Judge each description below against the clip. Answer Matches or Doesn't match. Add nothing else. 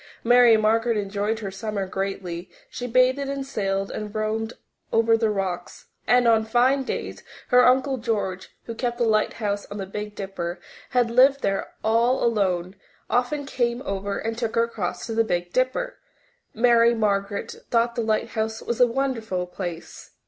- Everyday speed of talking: Matches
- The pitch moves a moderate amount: Matches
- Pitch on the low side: Doesn't match